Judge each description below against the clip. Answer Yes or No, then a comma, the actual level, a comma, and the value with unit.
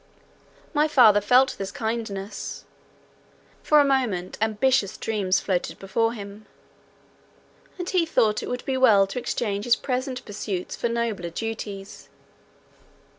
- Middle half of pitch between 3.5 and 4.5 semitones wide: Yes, average, 4.1 semitones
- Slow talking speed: Yes, slow, 130 wpm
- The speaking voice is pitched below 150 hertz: No, high, 220 Hz